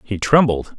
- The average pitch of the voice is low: Yes, low, 115 Hz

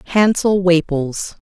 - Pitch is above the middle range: No, medium, 180 Hz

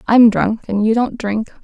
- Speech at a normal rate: No, fast, 220 wpm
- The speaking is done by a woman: Yes, female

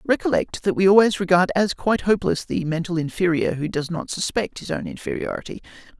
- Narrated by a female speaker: No, male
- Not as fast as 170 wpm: No, average, 180 wpm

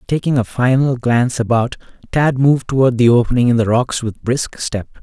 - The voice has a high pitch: No, low, 125 Hz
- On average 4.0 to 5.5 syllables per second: Yes, 5.4 syllables/s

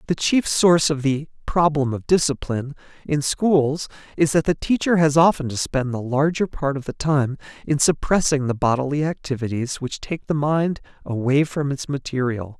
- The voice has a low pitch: No, medium, 145 Hz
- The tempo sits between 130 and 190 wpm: Yes, average, 175 wpm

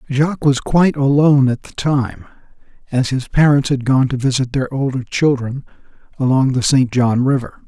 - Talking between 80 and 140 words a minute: No, average, 170 wpm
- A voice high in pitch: No, low, 135 Hz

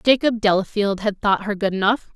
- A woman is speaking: Yes, female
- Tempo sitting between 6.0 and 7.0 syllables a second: No, 5.4 syllables/s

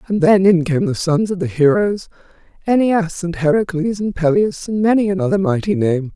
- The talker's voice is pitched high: Yes, high, 205 Hz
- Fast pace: No, average, 185 wpm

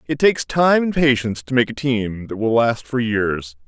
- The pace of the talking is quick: Yes, fast, 230 wpm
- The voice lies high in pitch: No, low, 125 Hz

